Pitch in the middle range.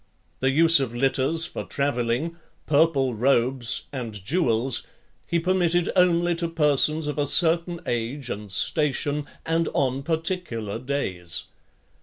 Yes: medium, 145 Hz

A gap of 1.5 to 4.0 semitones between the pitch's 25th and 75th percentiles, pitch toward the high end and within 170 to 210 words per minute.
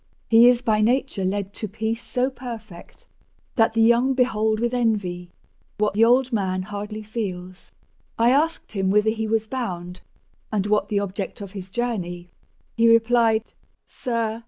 No: average, 2.9 semitones; high, 220 Hz; average, 160 wpm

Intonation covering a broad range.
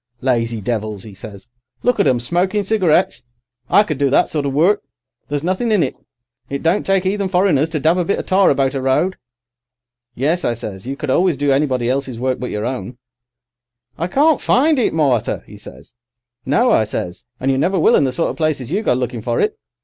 Yes: wide, 7.0 semitones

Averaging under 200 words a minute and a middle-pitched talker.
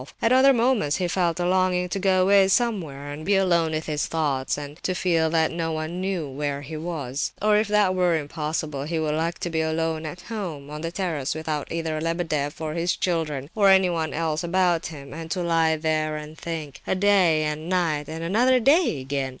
No: fast, 205 wpm; medium, 165 Hz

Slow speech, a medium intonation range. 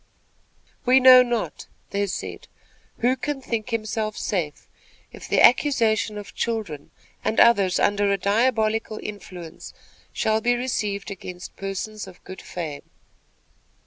Yes: slow, 125 wpm; average, 3.1 semitones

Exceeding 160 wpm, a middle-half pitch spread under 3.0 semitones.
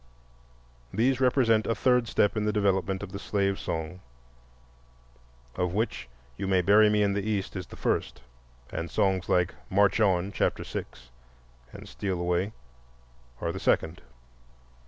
No: average, 150 wpm; narrow, 2.6 semitones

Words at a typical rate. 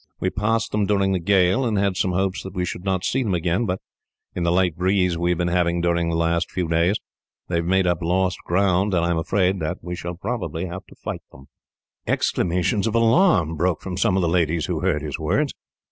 No: fast, 225 wpm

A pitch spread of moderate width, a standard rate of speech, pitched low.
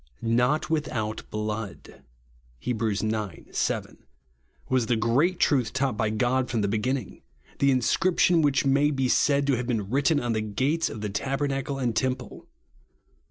Yes: average, 3.9 semitones; average, 150 wpm; low, 130 Hz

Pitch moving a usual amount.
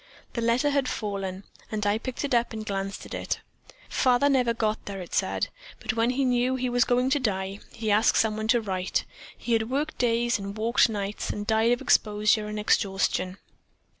Yes: average, 3.0 semitones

